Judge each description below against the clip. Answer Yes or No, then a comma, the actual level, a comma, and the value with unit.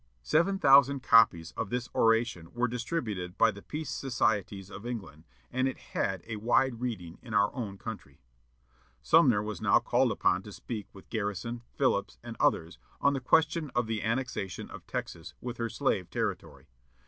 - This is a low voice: Yes, low, 115 Hz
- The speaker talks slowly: No, average, 170 wpm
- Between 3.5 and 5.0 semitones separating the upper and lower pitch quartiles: Yes, average, 4.4 semitones